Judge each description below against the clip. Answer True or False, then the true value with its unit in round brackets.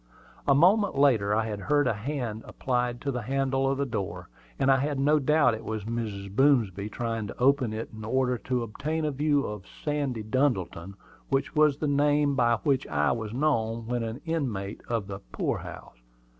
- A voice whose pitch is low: True (125 Hz)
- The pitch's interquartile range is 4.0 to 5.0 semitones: True (4.4 semitones)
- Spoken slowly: False (190 wpm)